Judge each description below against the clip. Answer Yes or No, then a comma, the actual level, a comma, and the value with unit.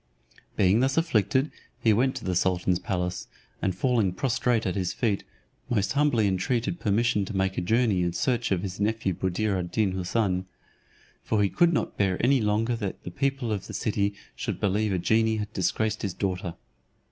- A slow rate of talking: No, average, 185 wpm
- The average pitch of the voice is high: No, low, 105 Hz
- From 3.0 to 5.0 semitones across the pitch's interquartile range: Yes, average, 3.9 semitones